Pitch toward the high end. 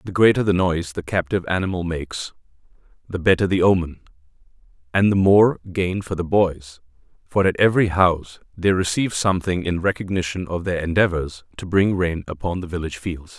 No: very low, 90 Hz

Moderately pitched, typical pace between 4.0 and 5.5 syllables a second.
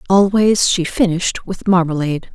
Yes: medium, 180 Hz; 5.1 syllables/s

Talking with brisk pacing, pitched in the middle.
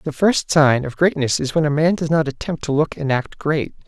Yes: fast, 265 wpm; medium, 150 Hz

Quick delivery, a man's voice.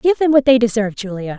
No: fast, 260 wpm; female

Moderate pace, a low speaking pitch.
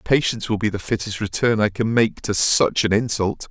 No: fast, 225 wpm; low, 105 Hz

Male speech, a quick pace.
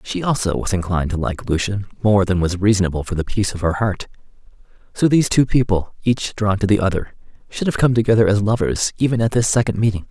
Yes: male; fast, 220 wpm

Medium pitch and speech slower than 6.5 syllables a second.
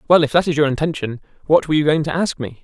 No: medium, 150 Hz; 7.4 syllables/s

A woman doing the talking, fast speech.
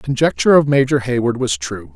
No: male; fast, 215 wpm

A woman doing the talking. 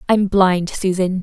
Yes: female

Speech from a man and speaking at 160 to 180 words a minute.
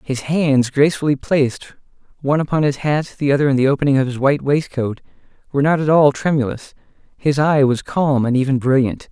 No: male; average, 190 wpm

